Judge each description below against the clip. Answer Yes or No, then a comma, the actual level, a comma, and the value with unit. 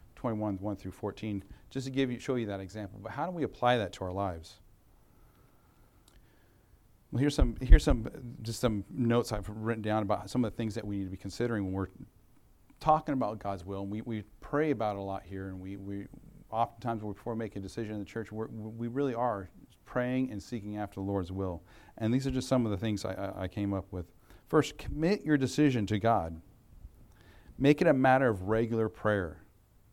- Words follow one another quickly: Yes, fast, 215 wpm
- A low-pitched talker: Yes, low, 110 Hz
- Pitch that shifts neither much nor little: Yes, average, 3.6 semitones